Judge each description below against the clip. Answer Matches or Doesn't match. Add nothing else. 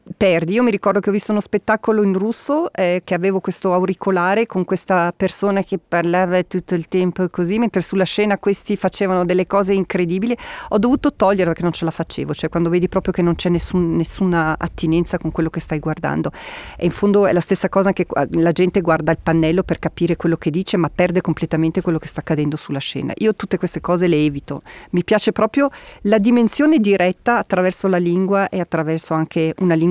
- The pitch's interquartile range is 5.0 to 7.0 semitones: Doesn't match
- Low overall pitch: Doesn't match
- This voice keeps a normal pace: Doesn't match